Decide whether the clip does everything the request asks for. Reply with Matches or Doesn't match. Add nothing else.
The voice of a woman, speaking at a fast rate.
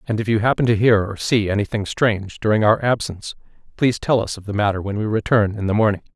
Doesn't match